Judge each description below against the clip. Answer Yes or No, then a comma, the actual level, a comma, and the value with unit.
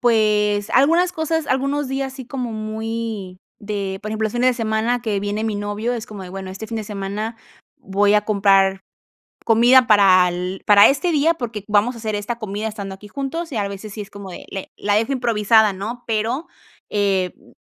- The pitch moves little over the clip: No, average, 3.1 semitones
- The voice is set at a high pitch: Yes, high, 215 Hz